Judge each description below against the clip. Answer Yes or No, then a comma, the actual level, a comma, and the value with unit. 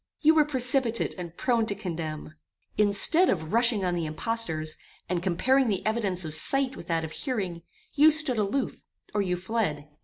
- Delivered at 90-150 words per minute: No, average, 175 wpm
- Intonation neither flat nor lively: No, wide, 6.8 semitones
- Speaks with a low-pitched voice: No, high, 205 Hz